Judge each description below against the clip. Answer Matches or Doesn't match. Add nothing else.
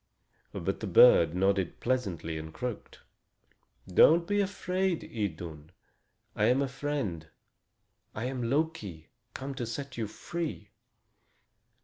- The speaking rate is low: Matches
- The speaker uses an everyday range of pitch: Doesn't match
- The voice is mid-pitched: Doesn't match